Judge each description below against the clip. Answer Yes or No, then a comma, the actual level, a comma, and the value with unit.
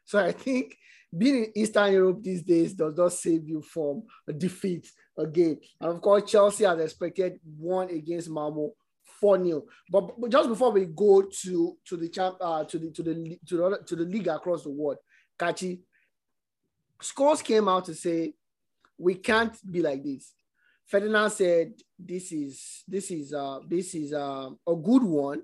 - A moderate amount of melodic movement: Yes, average, 3.5 semitones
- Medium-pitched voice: Yes, medium, 175 Hz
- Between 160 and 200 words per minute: No, average, 150 wpm